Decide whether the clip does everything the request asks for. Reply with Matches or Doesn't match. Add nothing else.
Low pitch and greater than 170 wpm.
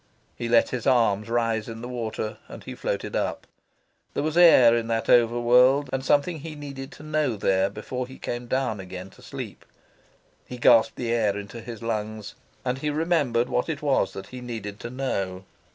Matches